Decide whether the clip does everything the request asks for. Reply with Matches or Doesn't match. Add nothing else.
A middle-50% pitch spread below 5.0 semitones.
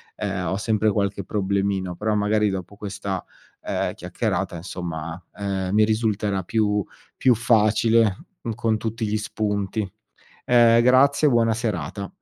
Matches